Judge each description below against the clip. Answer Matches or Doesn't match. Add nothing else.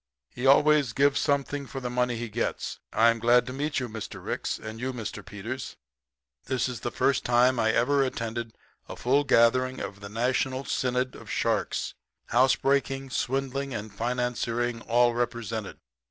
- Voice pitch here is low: Matches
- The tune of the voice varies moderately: Doesn't match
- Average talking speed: Matches